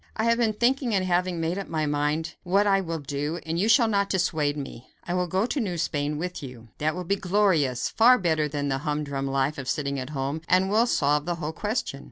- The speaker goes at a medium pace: No, fast, 240 wpm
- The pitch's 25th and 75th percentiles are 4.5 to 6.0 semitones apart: Yes, average, 5.1 semitones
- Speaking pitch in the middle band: Yes, medium, 165 Hz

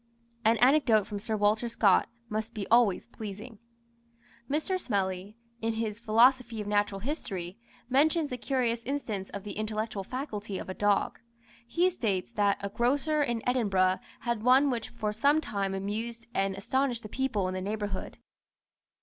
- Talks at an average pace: Yes, average, 160 wpm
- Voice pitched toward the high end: Yes, high, 220 Hz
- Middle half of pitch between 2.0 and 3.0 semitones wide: No, average, 3.6 semitones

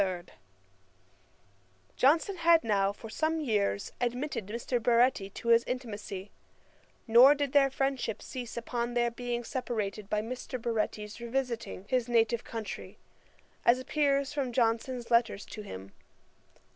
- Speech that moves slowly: Yes, slow, 125 wpm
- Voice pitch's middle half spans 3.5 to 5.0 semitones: No, average, 2.7 semitones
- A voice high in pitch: Yes, high, 235 Hz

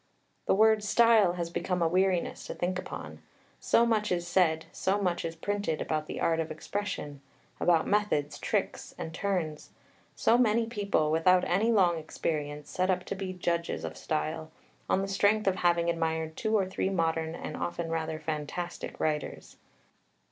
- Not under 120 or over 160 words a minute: No, average, 170 wpm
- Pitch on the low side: No, medium, 175 Hz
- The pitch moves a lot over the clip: No, average, 3.6 semitones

